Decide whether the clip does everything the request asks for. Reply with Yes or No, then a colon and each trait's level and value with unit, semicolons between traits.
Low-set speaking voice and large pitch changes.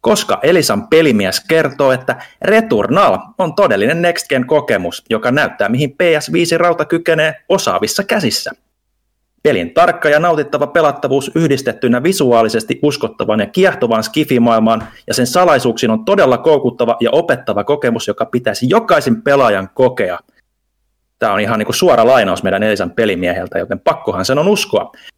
No: medium, 145 Hz; wide, 6.0 semitones